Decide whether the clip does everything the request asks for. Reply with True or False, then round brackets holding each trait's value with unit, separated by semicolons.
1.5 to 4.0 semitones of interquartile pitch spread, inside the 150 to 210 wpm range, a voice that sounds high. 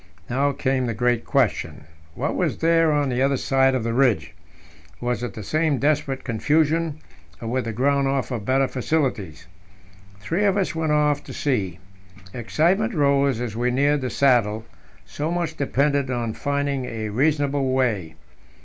False (3.4 semitones; 160 wpm; 135 Hz)